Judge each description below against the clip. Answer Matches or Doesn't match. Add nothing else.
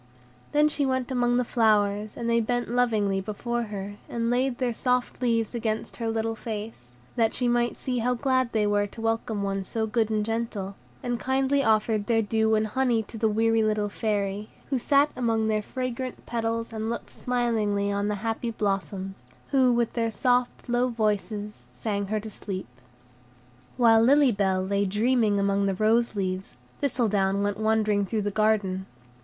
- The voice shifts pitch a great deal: Doesn't match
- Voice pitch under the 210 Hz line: Doesn't match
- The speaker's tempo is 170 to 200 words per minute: Matches